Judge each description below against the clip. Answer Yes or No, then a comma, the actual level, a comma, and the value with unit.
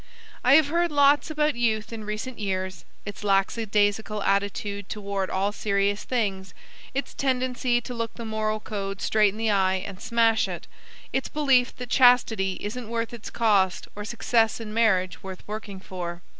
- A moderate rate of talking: Yes, average, 165 wpm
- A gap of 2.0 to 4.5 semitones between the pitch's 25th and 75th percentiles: Yes, average, 3.3 semitones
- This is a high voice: Yes, high, 215 Hz